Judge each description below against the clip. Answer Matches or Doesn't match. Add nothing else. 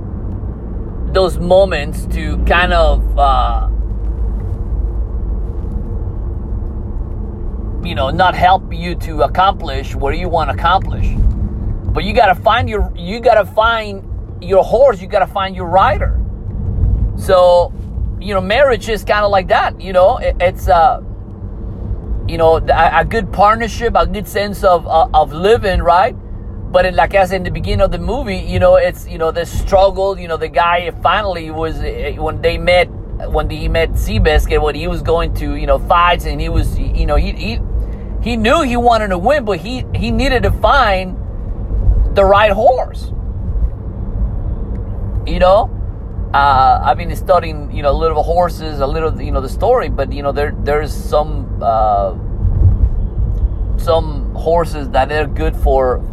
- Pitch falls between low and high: Doesn't match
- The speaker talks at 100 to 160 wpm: Doesn't match